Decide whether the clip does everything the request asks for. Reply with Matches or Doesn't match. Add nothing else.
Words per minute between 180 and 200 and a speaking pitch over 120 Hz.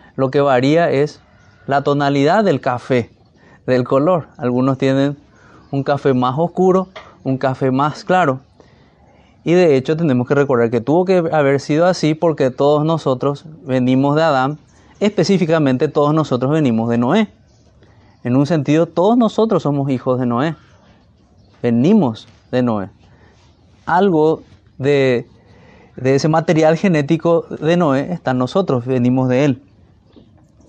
Doesn't match